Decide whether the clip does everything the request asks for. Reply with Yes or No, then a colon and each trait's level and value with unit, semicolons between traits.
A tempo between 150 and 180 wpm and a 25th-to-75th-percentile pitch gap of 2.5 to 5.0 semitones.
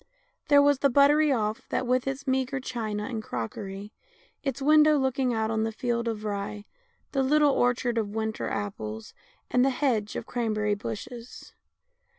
Yes: average, 160 wpm; average, 4.1 semitones